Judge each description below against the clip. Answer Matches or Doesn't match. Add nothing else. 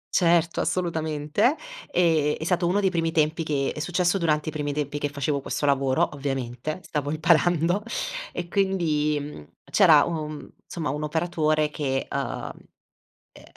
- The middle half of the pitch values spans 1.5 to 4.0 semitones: Matches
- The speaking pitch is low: Doesn't match